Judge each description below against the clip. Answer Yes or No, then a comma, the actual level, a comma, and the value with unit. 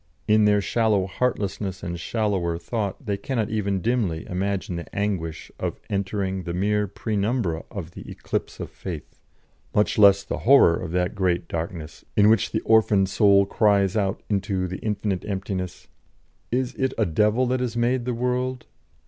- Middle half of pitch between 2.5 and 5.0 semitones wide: Yes, average, 3.2 semitones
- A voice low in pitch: Yes, low, 100 Hz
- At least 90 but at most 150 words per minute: No, average, 165 wpm